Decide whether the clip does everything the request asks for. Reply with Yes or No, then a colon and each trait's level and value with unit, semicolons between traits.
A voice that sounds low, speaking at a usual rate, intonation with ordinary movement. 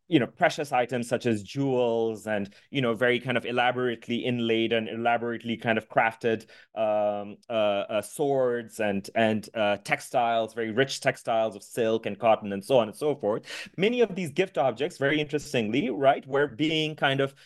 Yes: low, 120 Hz; average, 180 wpm; average, 3.5 semitones